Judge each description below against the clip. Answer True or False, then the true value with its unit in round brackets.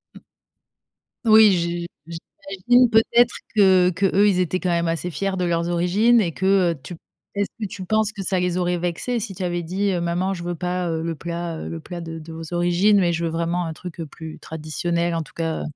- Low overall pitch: False (175 Hz)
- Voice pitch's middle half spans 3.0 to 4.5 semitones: False (2.4 semitones)